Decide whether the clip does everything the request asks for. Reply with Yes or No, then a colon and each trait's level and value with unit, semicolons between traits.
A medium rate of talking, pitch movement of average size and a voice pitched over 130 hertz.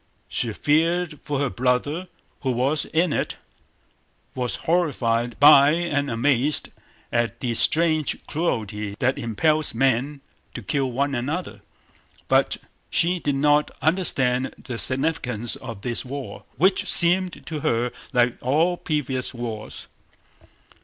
No: slow, 125 wpm; average, 4.4 semitones; medium, 140 Hz